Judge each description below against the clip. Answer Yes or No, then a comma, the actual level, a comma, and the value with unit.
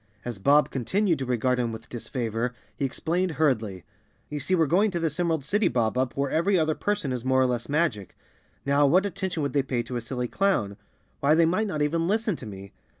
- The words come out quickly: Yes, fast, 225 wpm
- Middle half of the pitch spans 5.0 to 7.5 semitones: Yes, wide, 5.6 semitones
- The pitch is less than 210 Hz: Yes, medium, 140 Hz